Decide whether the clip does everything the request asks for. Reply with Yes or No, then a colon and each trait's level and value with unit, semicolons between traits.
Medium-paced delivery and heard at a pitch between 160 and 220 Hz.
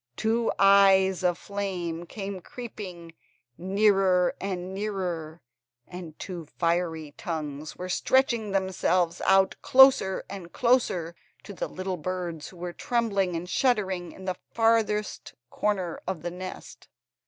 No: slow, 120 wpm; medium, 185 Hz